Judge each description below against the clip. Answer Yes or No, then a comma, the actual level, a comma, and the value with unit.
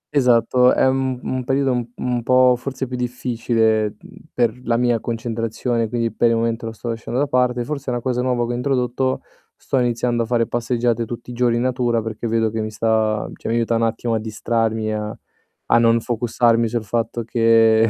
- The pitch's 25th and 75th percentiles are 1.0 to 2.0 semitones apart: Yes, narrow, 1.6 semitones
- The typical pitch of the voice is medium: No, low, 120 Hz